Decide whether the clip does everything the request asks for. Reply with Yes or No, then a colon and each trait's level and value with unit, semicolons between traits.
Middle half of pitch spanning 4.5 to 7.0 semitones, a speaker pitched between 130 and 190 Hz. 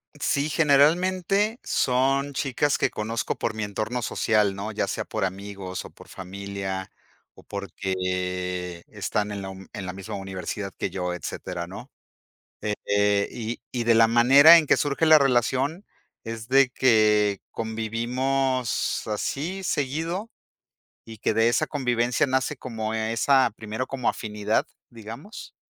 No: average, 5.1 semitones; low, 115 Hz